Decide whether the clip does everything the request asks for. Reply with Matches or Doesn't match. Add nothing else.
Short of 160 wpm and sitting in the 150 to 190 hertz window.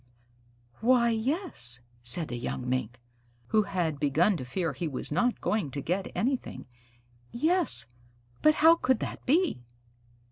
Matches